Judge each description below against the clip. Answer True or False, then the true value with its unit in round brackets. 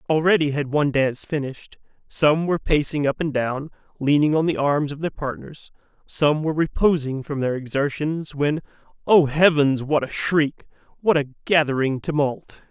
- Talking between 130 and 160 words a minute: True (155 wpm)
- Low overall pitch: False (150 Hz)